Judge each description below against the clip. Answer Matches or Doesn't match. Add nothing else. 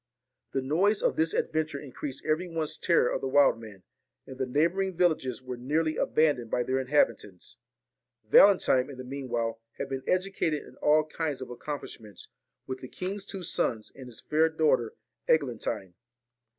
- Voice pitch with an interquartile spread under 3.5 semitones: Doesn't match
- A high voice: Doesn't match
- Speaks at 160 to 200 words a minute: Matches